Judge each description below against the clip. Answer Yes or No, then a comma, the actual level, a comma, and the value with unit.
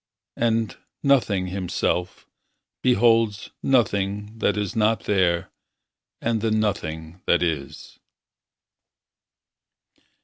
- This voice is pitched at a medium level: No, low, 105 Hz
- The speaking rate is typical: No, slow, 80 wpm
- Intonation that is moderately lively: Yes, average, 4.0 semitones